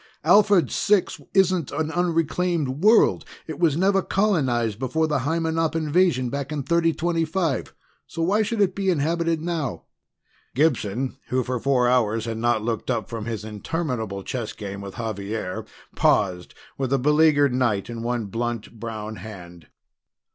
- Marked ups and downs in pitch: Yes, wide, 6.5 semitones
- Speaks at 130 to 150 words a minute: Yes, average, 145 wpm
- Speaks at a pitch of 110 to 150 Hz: Yes, low, 135 Hz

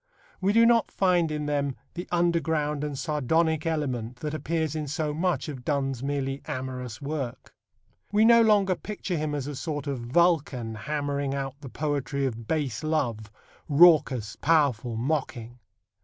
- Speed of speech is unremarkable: Yes, average, 155 wpm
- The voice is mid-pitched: Yes, medium, 145 Hz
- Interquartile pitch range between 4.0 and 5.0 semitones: No, average, 3.4 semitones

